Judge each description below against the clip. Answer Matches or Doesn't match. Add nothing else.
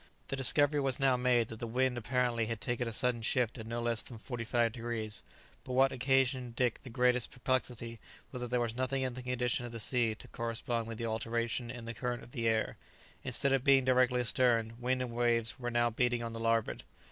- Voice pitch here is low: Matches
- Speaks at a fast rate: Matches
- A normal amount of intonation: Doesn't match